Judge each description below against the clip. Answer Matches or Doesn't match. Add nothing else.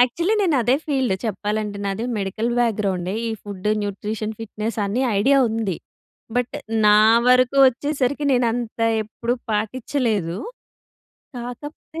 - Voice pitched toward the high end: Matches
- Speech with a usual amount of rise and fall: Matches